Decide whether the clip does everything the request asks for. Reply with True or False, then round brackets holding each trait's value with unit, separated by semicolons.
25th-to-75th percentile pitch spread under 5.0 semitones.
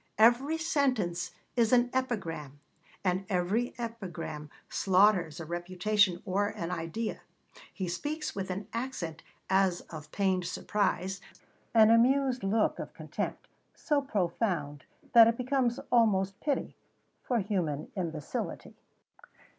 False (5.3 semitones)